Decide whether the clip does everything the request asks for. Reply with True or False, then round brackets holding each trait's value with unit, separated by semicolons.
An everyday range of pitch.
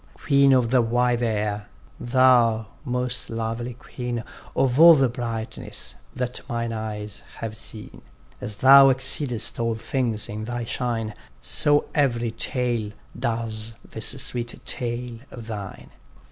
False (2.1 semitones)